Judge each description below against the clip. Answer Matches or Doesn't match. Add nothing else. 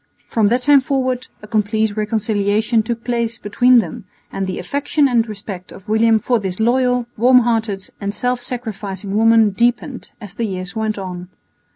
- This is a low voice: Doesn't match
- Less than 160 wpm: Doesn't match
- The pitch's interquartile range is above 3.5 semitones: Doesn't match